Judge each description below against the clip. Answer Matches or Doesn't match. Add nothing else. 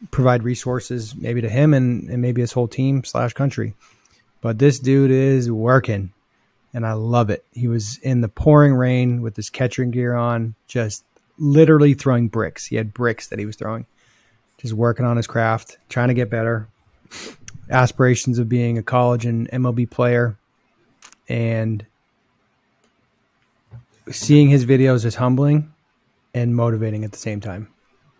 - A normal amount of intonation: Doesn't match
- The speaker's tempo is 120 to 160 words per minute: Matches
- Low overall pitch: Matches